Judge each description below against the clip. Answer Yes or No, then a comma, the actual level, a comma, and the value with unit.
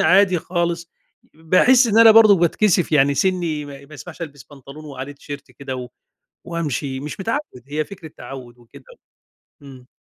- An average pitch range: Yes, average, 4.7 semitones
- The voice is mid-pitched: Yes, medium, 155 Hz